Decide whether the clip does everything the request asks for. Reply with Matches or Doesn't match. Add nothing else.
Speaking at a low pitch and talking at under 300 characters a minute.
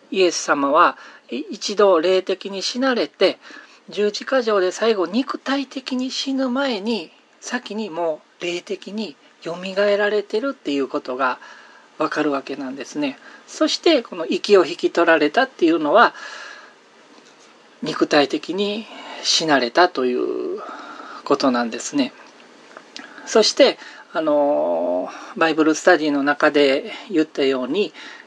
Doesn't match